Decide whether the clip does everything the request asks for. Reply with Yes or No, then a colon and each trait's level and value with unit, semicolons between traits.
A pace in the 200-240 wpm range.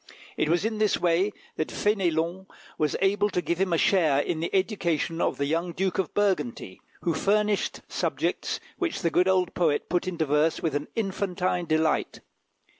No: average, 180 wpm